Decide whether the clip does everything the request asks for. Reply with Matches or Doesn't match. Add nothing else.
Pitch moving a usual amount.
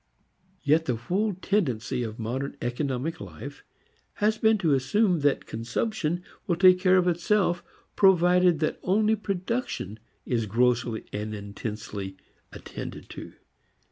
Doesn't match